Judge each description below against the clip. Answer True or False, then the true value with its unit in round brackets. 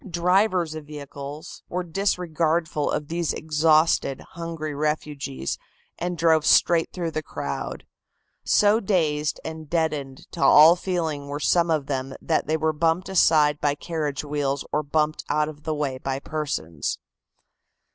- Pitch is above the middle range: False (155 Hz)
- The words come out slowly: False (145 wpm)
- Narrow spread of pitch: True (2.3 semitones)